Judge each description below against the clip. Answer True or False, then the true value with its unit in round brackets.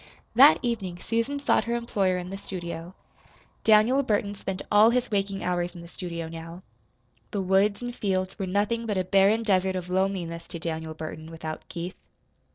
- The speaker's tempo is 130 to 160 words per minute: False (175 wpm)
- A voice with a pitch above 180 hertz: True (190 Hz)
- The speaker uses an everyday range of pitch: True (3.5 semitones)